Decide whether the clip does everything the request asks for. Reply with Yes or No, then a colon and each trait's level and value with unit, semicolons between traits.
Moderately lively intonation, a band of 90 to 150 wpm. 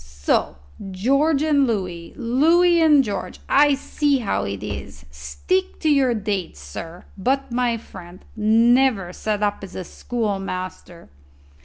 No: wide, 7.5 semitones; slow, 135 wpm